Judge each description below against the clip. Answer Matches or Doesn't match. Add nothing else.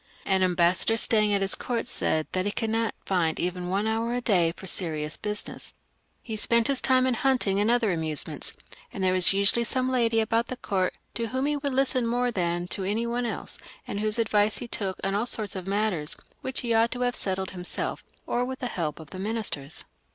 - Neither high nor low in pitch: Doesn't match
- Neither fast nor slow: Doesn't match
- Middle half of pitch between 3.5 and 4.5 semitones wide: Matches